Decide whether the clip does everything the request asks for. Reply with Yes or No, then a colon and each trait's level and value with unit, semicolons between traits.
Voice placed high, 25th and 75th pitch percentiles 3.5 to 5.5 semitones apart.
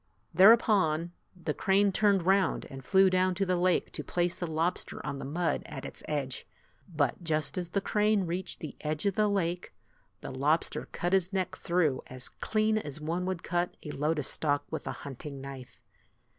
No: medium, 175 Hz; average, 3.9 semitones